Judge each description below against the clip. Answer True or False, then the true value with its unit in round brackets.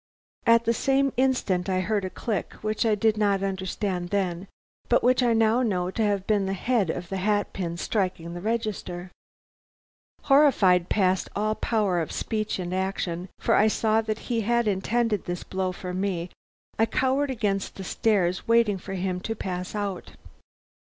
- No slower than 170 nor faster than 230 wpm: True (175 wpm)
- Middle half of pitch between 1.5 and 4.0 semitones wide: True (3.4 semitones)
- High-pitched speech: True (200 Hz)